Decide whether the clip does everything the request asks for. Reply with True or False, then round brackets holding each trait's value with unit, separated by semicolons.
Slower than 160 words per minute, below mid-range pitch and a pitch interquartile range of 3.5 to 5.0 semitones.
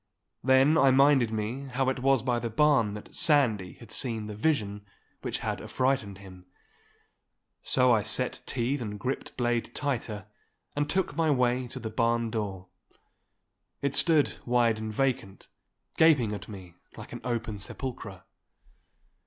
True (150 wpm; 120 Hz; 4.1 semitones)